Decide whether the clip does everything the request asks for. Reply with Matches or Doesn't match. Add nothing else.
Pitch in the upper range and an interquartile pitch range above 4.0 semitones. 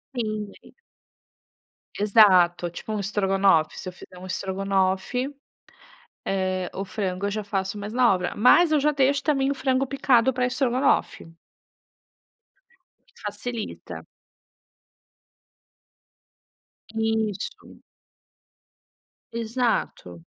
Matches